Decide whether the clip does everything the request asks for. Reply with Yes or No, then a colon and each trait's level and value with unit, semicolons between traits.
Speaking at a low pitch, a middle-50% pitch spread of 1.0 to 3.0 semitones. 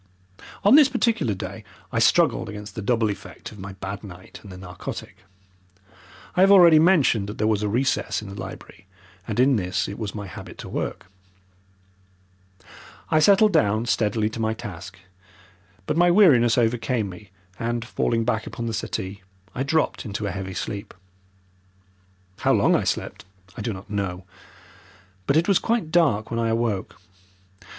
No: low, 110 Hz; average, 5.2 semitones